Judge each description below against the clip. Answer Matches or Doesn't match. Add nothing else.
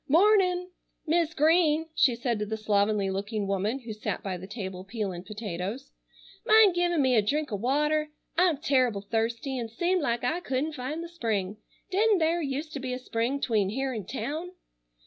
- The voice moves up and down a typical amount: Doesn't match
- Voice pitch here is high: Matches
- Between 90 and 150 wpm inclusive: Doesn't match